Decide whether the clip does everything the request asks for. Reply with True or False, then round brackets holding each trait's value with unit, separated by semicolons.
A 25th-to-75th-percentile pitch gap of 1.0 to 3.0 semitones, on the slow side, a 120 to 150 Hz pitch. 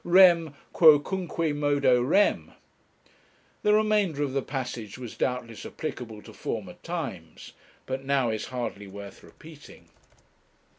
False (5.2 semitones; 115 wpm; 140 Hz)